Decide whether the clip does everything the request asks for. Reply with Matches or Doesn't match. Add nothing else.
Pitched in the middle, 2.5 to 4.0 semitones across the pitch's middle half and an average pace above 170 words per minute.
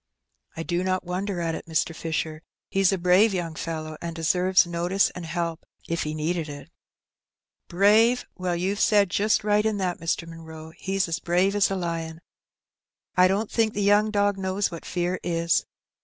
Matches